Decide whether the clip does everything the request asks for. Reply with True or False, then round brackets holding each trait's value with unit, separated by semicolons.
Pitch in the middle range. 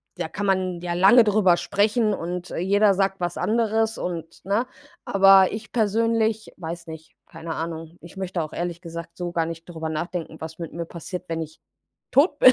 True (180 Hz)